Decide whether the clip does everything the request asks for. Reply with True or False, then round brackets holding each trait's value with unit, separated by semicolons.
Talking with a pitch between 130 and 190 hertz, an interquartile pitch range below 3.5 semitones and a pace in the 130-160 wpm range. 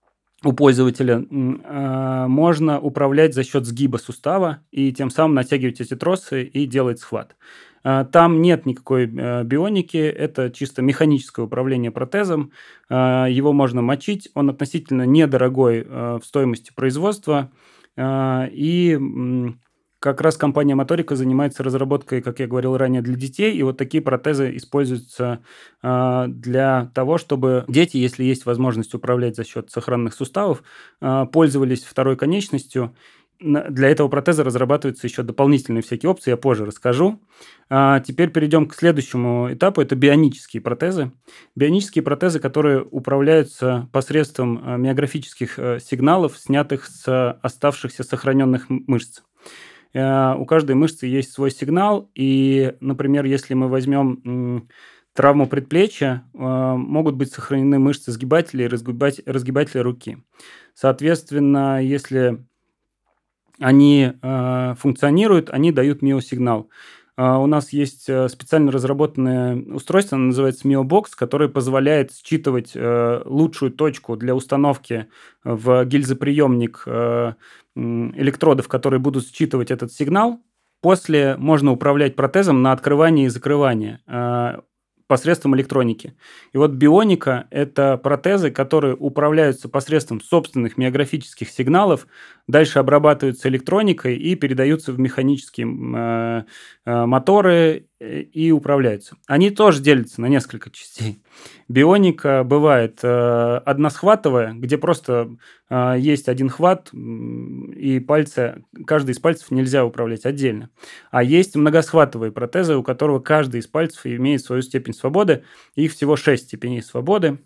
False (135 Hz; 2.8 semitones; 115 wpm)